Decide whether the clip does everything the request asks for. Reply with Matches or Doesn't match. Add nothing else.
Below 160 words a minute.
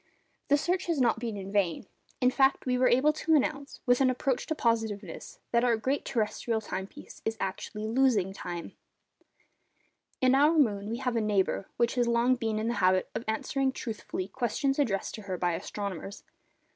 Doesn't match